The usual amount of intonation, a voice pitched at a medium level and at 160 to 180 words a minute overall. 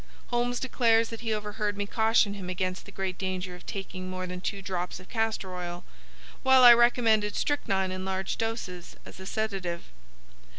No: average, 3.5 semitones; high, 200 Hz; average, 175 wpm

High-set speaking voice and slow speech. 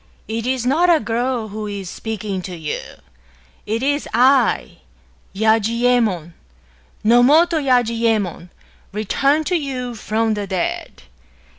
Yes: high, 230 Hz; slow, 125 wpm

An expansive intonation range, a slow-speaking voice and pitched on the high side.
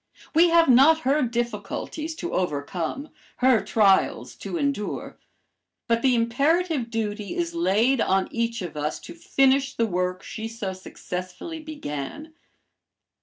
Yes: wide, 7.5 semitones; slow, 130 wpm; high, 235 Hz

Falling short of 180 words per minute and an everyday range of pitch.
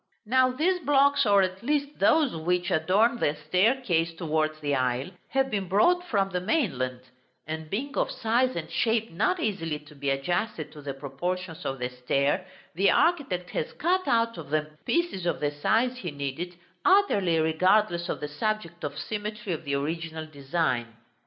No: average, 170 wpm; wide, 7.2 semitones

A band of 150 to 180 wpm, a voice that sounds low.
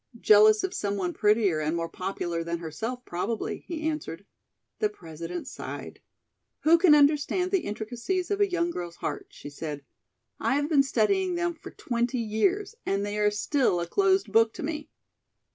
No: average, 175 wpm; high, 230 Hz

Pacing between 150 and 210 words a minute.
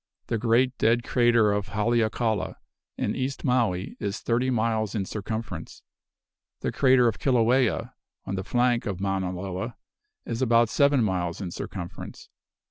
No: average, 140 wpm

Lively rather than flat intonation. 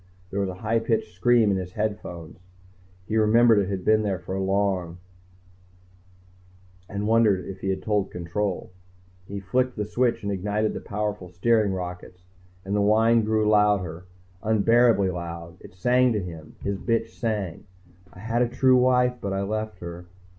No: average, 3.3 semitones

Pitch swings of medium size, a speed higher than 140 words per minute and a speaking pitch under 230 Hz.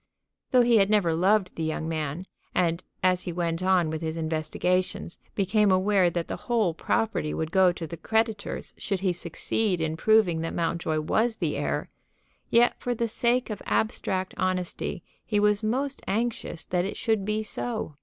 Yes: average, 4.5 semitones; average, 175 wpm; medium, 185 Hz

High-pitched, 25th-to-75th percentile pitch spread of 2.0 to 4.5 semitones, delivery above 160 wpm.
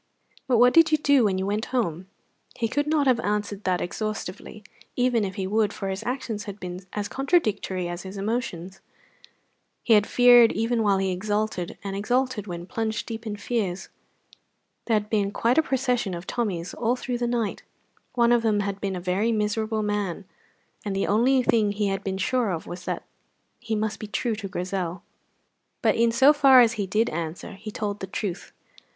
Yes: high, 210 Hz; average, 3.6 semitones; average, 195 wpm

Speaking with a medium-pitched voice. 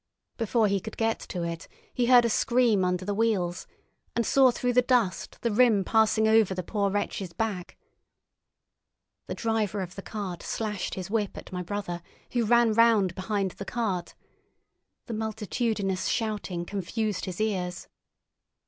No: high, 210 Hz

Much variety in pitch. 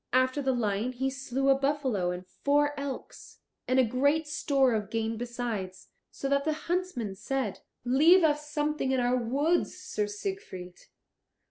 No: average, 4.2 semitones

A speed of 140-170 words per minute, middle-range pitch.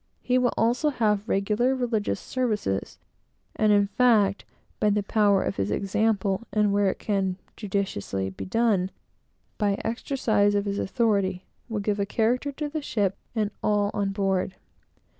No: average, 160 wpm; high, 205 Hz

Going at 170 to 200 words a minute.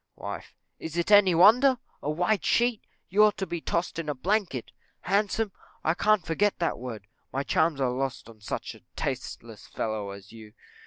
Yes: average, 180 wpm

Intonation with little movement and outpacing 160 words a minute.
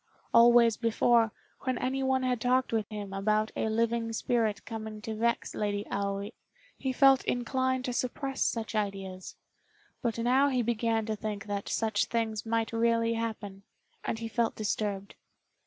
No: narrow, 2.2 semitones; average, 155 wpm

